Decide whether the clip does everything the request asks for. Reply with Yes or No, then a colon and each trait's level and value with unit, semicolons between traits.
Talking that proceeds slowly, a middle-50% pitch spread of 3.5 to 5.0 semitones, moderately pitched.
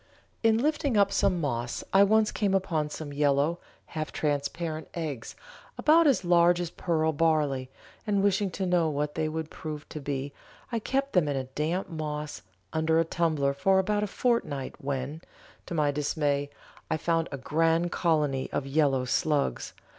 No: average, 165 wpm; average, 4.2 semitones; medium, 160 Hz